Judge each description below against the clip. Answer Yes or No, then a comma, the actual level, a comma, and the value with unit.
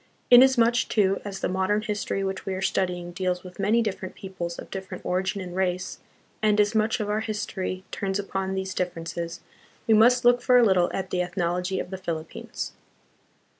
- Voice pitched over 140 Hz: Yes, high, 190 Hz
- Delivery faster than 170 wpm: Yes, average, 190 wpm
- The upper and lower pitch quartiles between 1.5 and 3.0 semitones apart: Yes, narrow, 2.6 semitones